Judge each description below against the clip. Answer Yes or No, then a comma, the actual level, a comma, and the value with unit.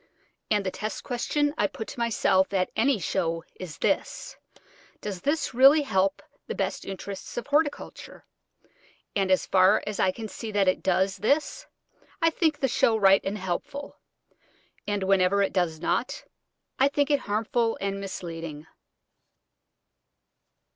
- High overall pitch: Yes, high, 205 Hz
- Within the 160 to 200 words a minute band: No, average, 145 wpm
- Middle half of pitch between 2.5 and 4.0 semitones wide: No, average, 5.3 semitones